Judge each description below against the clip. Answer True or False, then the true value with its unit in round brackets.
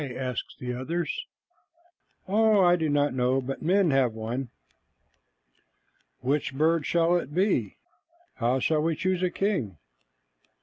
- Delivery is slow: True (130 wpm)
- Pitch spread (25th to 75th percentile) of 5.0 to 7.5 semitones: True (5.3 semitones)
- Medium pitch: True (150 Hz)